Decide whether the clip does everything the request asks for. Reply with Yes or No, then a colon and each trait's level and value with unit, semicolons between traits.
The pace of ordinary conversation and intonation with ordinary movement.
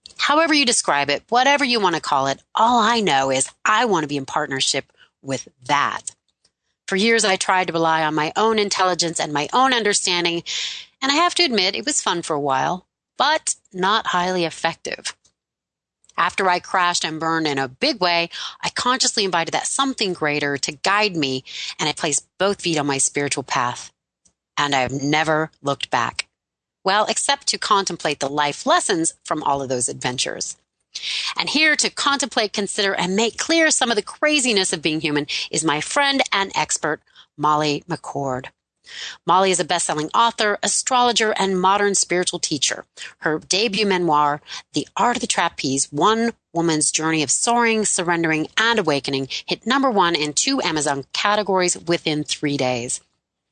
No: average, 175 wpm; wide, 6.6 semitones